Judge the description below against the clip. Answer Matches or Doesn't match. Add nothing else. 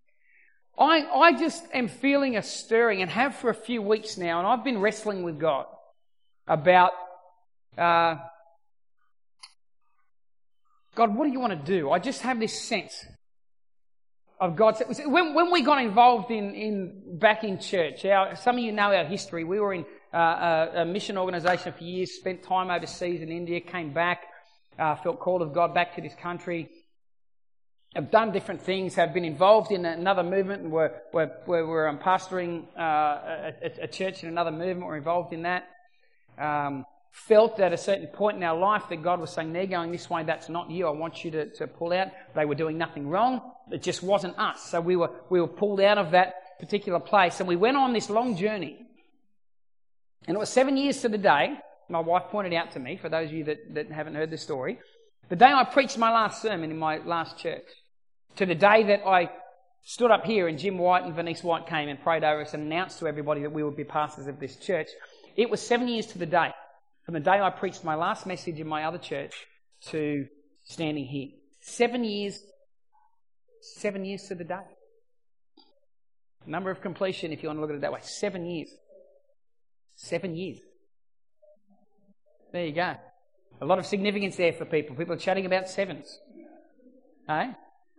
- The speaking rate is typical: Matches